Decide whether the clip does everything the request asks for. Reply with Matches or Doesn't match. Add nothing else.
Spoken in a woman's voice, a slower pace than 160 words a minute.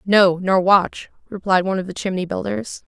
Doesn't match